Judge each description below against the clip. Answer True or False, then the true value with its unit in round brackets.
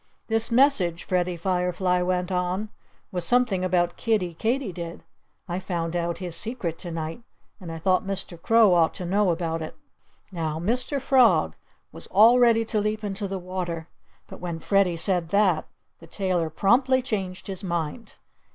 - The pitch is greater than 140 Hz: True (185 Hz)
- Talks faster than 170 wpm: False (160 wpm)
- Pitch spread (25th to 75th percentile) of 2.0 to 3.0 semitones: False (3.8 semitones)